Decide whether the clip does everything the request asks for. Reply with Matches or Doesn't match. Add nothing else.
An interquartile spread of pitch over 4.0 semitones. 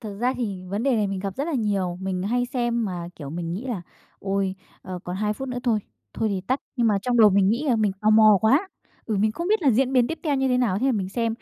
Matches